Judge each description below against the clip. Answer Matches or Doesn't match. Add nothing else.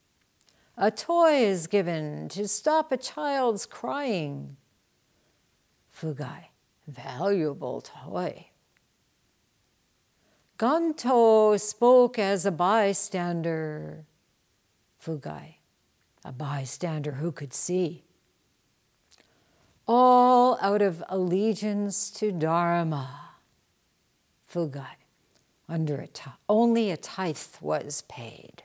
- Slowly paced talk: Matches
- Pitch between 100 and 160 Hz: Doesn't match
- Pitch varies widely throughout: Matches